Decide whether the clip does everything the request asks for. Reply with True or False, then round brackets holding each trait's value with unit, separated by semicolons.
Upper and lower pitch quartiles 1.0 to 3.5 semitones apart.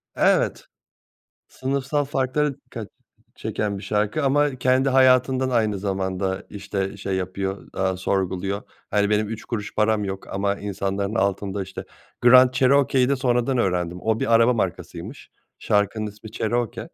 False (4.7 semitones)